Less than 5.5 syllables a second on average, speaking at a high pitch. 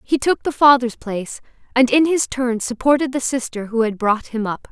Yes: 5.2 syllables/s; very high, 250 Hz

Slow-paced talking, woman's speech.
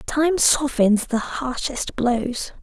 Yes: slow, 115 wpm; female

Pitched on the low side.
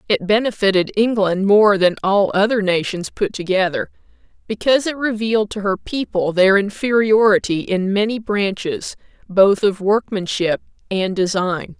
No: high, 200 Hz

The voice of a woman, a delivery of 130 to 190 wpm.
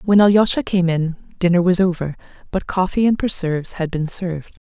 Yes: female; average, 180 wpm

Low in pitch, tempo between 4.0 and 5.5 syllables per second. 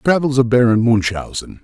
Yes: low, 120 Hz; 5.2 syllables/s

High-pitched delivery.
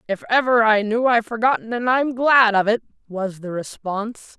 Yes: high, 225 Hz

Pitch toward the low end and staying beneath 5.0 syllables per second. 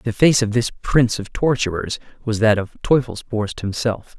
Yes: low, 115 Hz; 4.8 syllables/s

